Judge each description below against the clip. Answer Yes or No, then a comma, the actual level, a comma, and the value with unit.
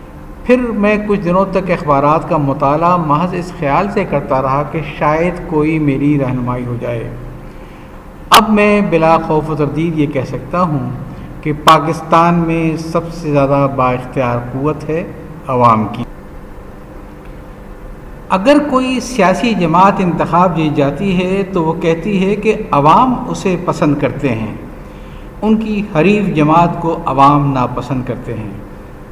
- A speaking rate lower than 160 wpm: Yes, average, 145 wpm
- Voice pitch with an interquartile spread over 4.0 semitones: Yes, average, 4.6 semitones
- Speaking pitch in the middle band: Yes, medium, 160 Hz